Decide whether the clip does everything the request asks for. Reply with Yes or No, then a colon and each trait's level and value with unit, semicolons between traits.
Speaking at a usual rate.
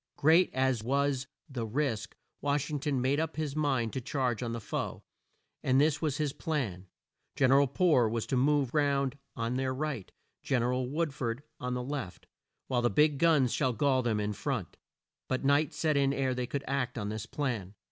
No: fast, 210 wpm